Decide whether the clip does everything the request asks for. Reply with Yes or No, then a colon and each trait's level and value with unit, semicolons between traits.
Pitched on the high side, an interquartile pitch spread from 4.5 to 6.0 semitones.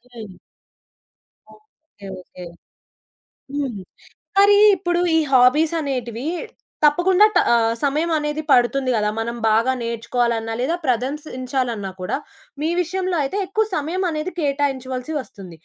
Yes: very high, 270 Hz; average, 5.3 semitones